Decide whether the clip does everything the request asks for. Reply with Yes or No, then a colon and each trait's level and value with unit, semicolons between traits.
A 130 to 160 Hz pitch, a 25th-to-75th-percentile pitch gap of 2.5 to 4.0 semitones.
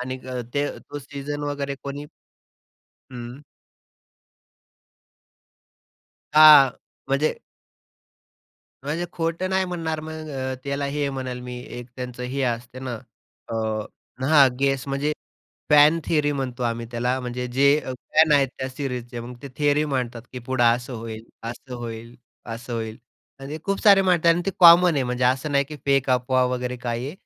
Yes: low, 135 Hz; average, 3.0 semitones